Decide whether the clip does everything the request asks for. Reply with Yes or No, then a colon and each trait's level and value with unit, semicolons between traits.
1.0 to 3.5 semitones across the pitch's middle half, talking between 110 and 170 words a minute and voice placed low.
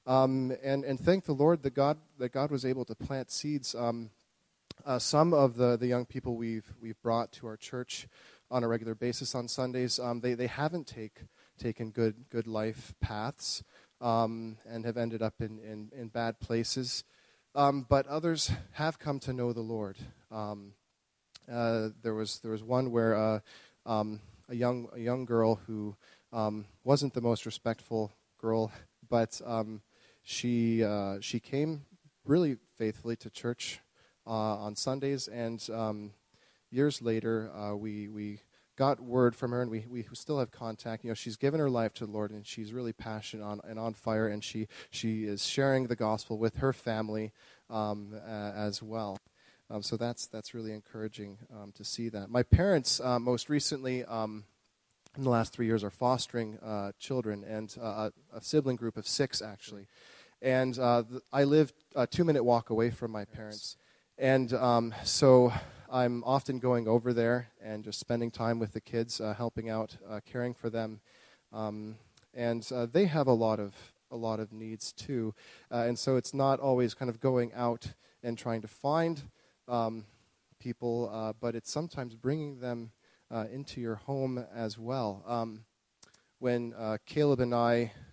No: narrow, 2.5 semitones; average, 180 wpm; low, 115 Hz